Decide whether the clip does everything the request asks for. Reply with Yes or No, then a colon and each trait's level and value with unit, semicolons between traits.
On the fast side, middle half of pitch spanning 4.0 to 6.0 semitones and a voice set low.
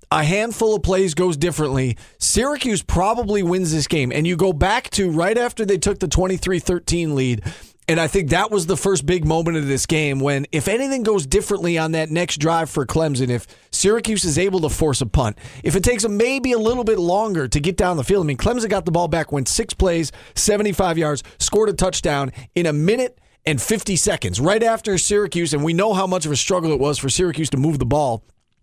No: fast, 225 wpm; wide, 5.4 semitones; medium, 175 Hz